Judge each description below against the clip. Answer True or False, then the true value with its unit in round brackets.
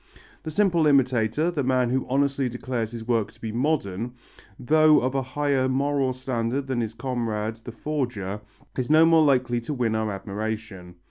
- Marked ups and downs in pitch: False (3.9 semitones)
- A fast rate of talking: False (175 wpm)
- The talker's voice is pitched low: True (125 Hz)